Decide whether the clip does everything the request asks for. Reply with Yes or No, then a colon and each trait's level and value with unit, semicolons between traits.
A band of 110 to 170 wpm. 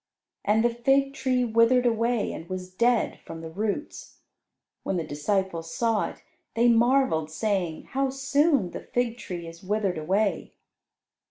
Yes: average, 150 wpm